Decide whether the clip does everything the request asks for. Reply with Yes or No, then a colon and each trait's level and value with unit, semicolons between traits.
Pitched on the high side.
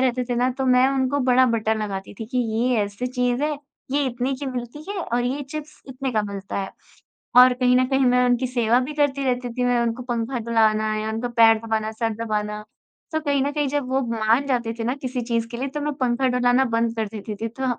Yes: very high, 250 Hz